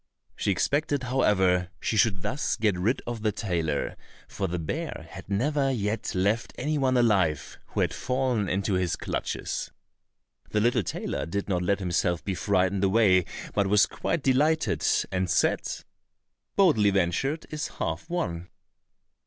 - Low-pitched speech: Yes, low, 100 Hz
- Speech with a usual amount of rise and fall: No, wide, 5.8 semitones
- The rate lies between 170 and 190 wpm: No, average, 150 wpm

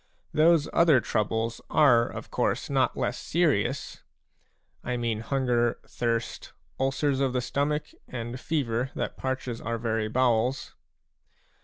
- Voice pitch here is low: Yes, low, 125 Hz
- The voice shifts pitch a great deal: No, average, 2.8 semitones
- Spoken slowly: Yes, slow, 125 wpm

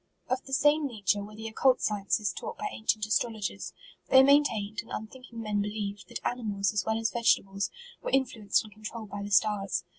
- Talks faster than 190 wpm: Yes, average, 200 wpm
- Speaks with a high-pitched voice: Yes, high, 215 Hz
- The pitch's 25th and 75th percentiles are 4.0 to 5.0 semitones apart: No, average, 2.9 semitones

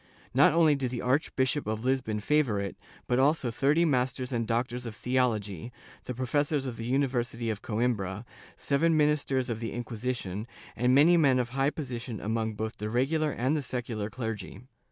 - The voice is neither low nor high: No, low, 125 Hz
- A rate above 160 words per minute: Yes, average, 175 wpm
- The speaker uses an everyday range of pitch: Yes, average, 3.5 semitones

